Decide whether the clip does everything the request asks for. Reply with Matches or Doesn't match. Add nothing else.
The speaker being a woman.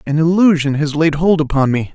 Doesn't match